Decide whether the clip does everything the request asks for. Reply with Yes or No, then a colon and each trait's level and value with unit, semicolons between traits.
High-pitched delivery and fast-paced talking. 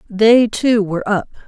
No: high, 215 Hz; average, 165 wpm